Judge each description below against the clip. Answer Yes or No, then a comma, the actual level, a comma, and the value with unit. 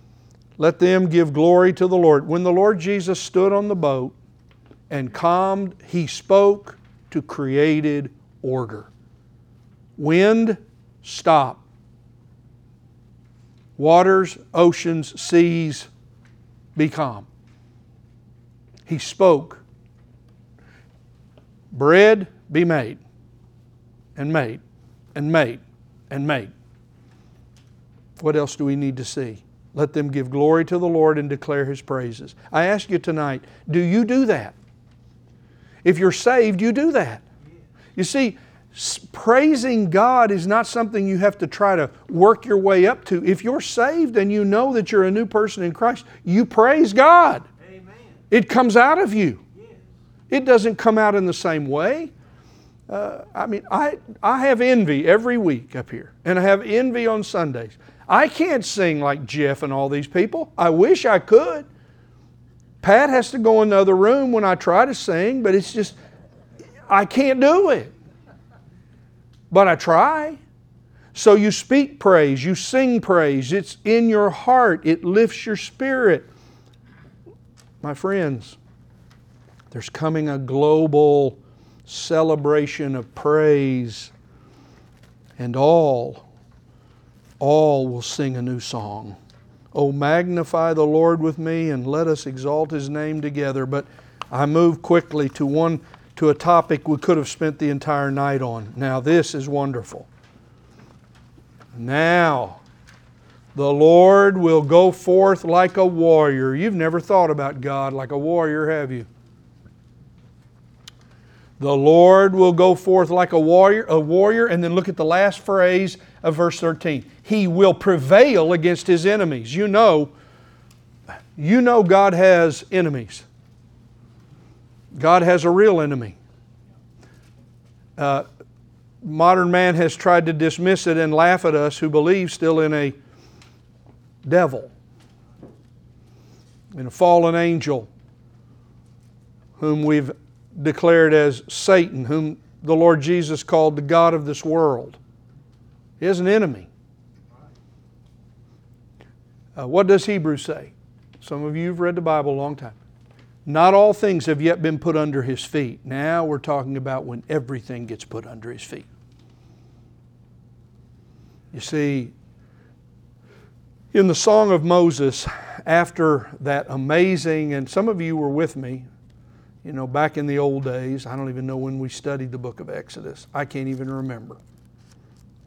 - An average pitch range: No, wide, 6.1 semitones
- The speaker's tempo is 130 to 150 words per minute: Yes, average, 140 wpm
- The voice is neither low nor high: Yes, medium, 155 Hz